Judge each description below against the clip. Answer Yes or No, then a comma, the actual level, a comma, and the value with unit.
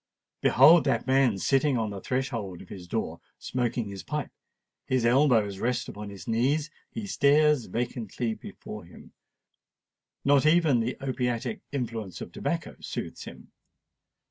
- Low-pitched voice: Yes, low, 125 Hz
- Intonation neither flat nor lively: Yes, average, 4.0 semitones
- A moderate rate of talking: No, slow, 125 wpm